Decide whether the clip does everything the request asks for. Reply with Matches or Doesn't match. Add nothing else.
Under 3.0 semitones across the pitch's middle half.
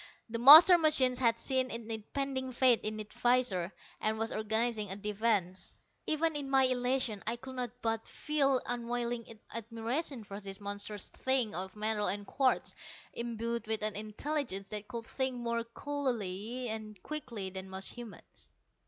Doesn't match